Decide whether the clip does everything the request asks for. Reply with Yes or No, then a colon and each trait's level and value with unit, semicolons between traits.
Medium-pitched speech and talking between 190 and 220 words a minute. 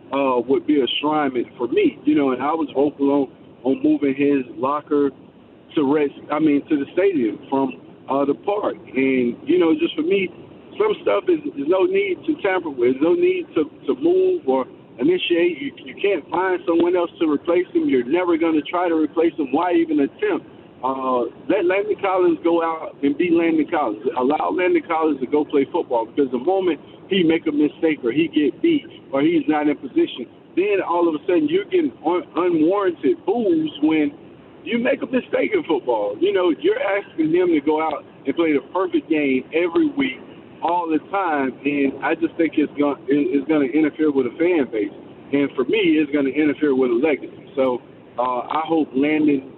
Yes: medium, 170 Hz; average, 200 wpm